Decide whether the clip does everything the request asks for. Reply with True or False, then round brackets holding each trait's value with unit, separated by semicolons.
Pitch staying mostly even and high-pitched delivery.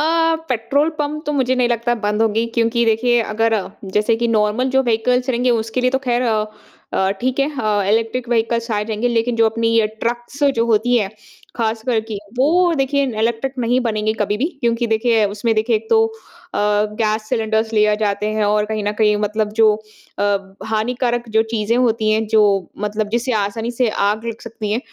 True (2.1 semitones; 230 Hz)